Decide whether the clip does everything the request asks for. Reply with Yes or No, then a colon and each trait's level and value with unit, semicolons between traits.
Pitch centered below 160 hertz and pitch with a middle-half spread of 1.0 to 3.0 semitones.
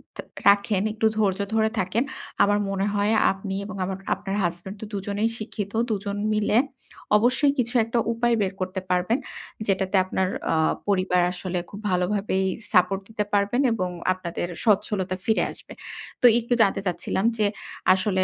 No: high, 200 Hz; narrow, 2.4 semitones